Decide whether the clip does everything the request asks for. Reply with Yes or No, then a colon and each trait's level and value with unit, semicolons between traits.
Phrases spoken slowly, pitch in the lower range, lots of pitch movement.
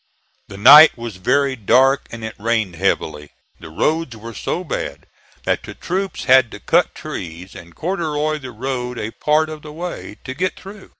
No: average, 180 wpm; low, 130 Hz; wide, 6.4 semitones